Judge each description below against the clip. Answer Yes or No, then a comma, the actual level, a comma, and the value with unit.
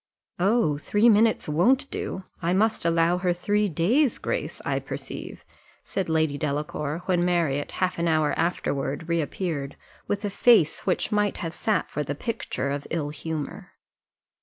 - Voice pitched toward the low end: No, medium, 170 Hz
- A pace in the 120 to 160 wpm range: Yes, average, 155 wpm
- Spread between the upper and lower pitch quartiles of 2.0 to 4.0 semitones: No, average, 5.2 semitones